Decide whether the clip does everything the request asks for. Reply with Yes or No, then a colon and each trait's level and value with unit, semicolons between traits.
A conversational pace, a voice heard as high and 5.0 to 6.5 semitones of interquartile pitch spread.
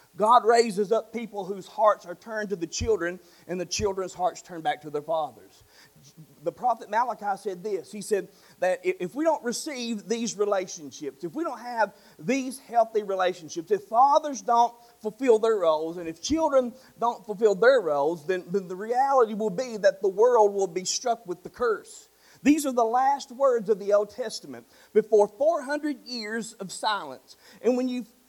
Yes: average, 180 wpm; high, 220 Hz; average, 5.3 semitones